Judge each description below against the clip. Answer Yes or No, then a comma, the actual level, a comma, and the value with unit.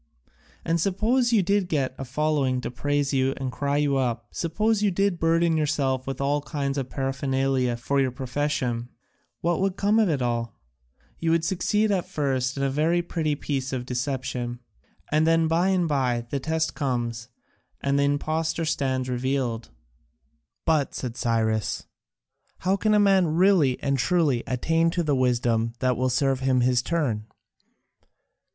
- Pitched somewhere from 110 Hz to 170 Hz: Yes, medium, 140 Hz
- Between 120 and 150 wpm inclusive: No, average, 160 wpm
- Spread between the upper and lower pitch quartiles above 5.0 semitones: No, average, 4.4 semitones